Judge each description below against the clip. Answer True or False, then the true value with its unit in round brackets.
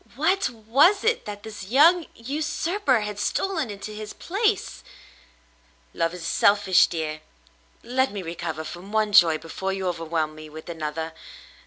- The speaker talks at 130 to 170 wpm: True (145 wpm)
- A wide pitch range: True (8.4 semitones)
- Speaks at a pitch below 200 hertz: False (205 Hz)